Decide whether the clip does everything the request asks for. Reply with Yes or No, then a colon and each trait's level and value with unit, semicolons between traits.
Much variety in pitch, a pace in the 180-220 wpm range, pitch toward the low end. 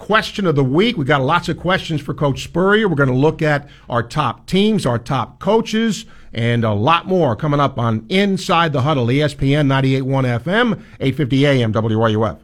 No: wide, 5.9 semitones; average, 190 wpm; medium, 145 Hz